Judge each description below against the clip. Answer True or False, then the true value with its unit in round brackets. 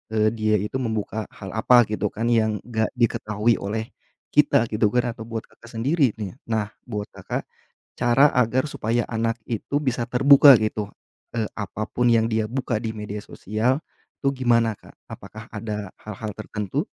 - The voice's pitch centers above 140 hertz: False (115 Hz)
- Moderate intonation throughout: False (2.3 semitones)